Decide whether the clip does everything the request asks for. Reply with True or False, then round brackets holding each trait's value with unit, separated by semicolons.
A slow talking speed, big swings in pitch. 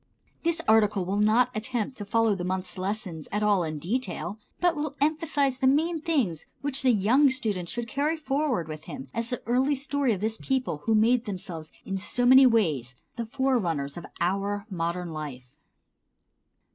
False (175 wpm; 6.5 semitones)